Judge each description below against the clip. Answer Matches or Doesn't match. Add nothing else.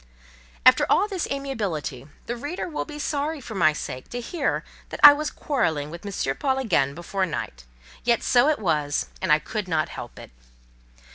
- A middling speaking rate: Matches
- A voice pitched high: Matches